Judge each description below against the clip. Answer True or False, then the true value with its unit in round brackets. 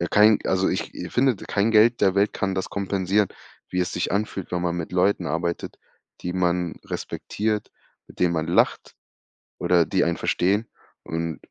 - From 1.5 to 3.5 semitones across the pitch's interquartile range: True (2.8 semitones)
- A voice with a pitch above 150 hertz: False (95 Hz)